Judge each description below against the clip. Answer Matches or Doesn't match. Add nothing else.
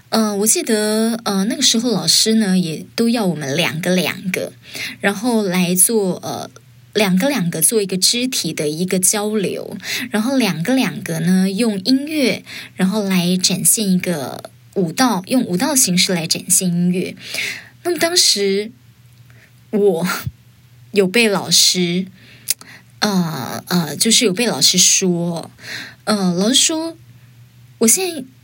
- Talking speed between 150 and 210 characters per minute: Matches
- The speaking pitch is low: Doesn't match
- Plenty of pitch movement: Doesn't match